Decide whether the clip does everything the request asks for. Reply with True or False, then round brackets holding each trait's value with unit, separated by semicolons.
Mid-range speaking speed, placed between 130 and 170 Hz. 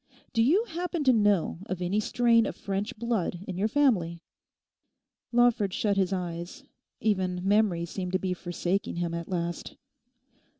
False (155 wpm; 195 Hz)